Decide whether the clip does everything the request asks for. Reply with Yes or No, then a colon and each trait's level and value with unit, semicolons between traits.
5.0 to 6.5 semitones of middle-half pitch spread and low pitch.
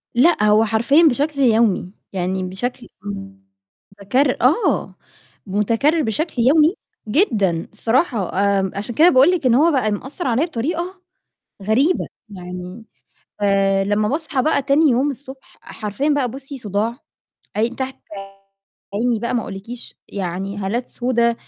No: wide, 5.5 semitones; high, 235 Hz